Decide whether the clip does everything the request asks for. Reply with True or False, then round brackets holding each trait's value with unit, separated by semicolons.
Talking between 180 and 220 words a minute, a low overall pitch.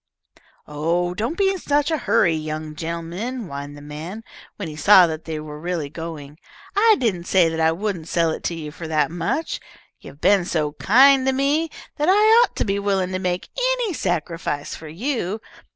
False (195 wpm; 175 Hz)